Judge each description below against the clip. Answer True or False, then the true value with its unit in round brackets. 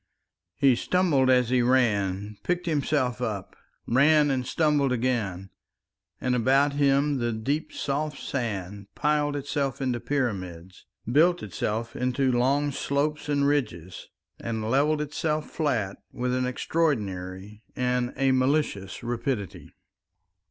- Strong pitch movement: False (4.5 semitones)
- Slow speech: True (120 wpm)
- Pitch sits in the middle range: False (130 Hz)